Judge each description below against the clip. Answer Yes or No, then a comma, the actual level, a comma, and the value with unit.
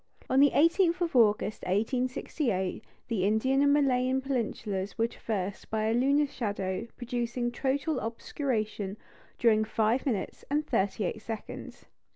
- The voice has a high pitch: Yes, high, 235 Hz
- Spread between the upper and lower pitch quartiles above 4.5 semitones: No, average, 4.0 semitones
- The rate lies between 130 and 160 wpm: Yes, slow, 135 wpm